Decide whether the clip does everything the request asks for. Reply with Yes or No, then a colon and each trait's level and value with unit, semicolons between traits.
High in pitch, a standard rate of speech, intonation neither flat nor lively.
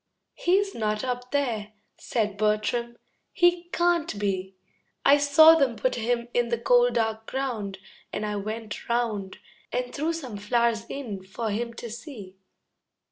Yes: high, 235 Hz; average, 145 wpm; average, 3.7 semitones